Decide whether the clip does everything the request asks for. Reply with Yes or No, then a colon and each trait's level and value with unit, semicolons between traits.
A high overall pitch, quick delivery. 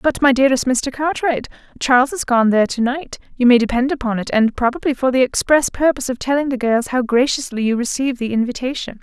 Yes: very high, 255 Hz; fast, 215 wpm